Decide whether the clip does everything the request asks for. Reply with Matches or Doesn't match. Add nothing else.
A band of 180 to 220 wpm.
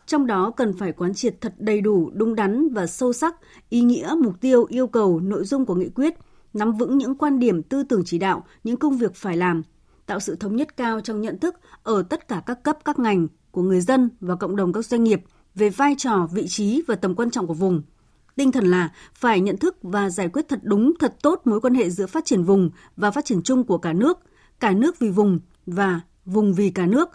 Doesn't match